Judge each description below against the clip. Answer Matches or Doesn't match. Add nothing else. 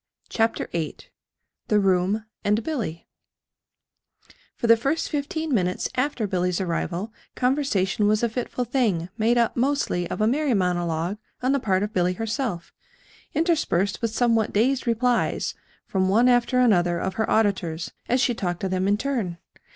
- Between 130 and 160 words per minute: Matches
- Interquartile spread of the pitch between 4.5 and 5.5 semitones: Matches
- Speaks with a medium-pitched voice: Doesn't match